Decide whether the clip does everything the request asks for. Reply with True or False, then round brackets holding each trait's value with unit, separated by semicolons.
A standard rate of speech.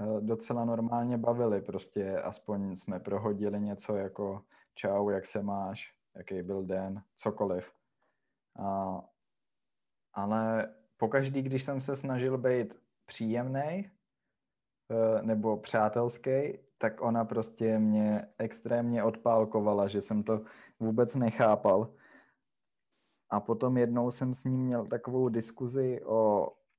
False (110 wpm)